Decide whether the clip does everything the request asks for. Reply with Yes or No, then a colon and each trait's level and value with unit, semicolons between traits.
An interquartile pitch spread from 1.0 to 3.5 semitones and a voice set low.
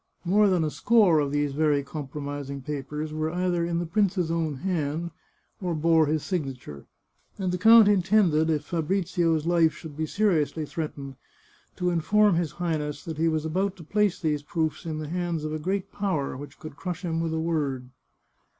No: average, 3.1 semitones; medium, 160 Hz